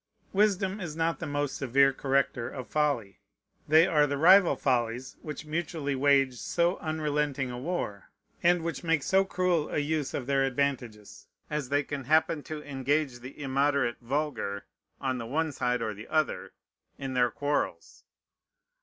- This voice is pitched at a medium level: Yes, medium, 145 Hz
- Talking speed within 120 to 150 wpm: No, average, 160 wpm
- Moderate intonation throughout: Yes, average, 3.3 semitones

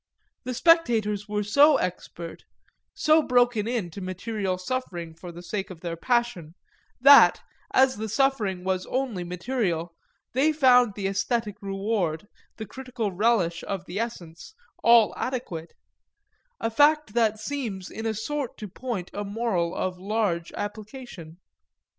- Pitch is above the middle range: Yes, high, 210 Hz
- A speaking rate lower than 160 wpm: Yes, average, 140 wpm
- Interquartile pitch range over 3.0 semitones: Yes, average, 5.1 semitones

